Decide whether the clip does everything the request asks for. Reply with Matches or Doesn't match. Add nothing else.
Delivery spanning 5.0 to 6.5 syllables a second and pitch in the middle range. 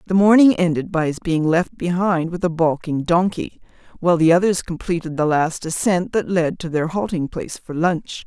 Matches